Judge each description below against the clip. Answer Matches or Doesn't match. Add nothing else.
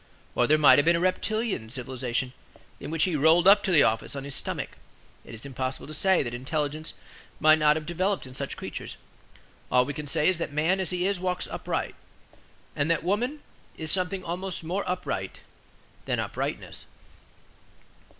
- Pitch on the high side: Doesn't match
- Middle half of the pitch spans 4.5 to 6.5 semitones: Matches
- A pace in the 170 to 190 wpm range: Matches